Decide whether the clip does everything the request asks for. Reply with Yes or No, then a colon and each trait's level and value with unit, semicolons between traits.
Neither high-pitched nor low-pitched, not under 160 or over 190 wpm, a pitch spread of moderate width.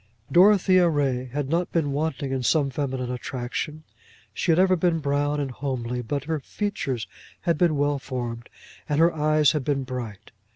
Yes: medium, 145 Hz; average, 170 wpm; average, 3.8 semitones